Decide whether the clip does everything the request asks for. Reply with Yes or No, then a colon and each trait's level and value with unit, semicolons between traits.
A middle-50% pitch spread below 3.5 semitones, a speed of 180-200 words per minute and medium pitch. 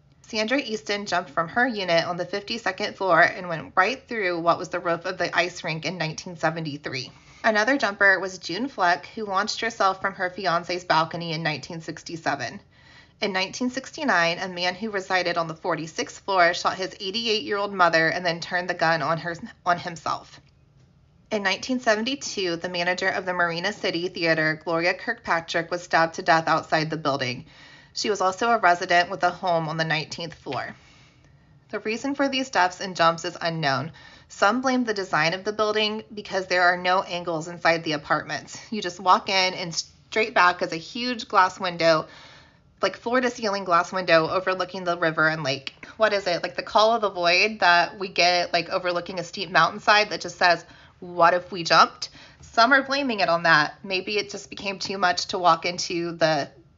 Yes: average, 3.1 semitones; average, 190 wpm; medium, 180 Hz